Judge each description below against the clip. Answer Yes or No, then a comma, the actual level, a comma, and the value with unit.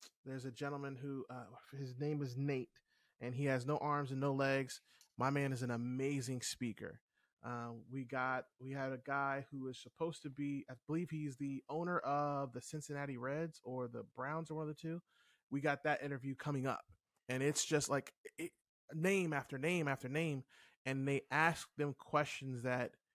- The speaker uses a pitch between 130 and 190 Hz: Yes, medium, 140 Hz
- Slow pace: No, average, 190 wpm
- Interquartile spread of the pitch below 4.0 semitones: Yes, narrow, 2.4 semitones